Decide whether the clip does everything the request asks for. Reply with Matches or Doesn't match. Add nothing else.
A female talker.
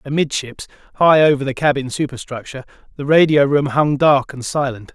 Doesn't match